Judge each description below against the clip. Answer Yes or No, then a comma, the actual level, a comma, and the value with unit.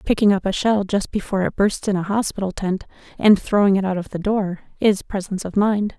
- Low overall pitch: No, high, 200 Hz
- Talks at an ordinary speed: No, fast, 230 wpm